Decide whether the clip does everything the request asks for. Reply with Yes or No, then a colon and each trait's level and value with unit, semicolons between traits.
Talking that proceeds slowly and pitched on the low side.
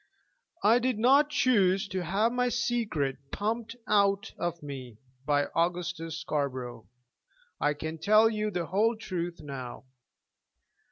No: slow, 125 wpm; medium, 185 Hz